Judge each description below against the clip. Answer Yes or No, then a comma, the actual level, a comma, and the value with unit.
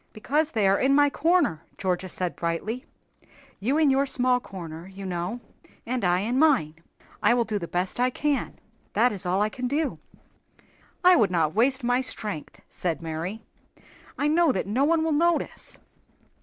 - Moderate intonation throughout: No, wide, 7.3 semitones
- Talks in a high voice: Yes, high, 235 Hz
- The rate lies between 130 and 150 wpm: No, average, 175 wpm